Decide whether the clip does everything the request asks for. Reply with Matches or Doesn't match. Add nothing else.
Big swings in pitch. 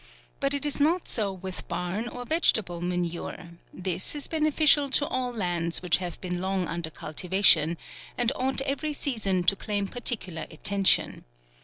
Matches